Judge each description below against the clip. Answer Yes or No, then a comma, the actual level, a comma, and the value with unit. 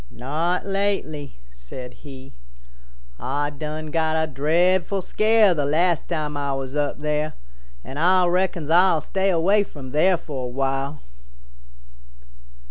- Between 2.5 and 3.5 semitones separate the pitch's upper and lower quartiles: No, average, 4.2 semitones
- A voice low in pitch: No, medium, 155 Hz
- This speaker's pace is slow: Yes, slow, 130 wpm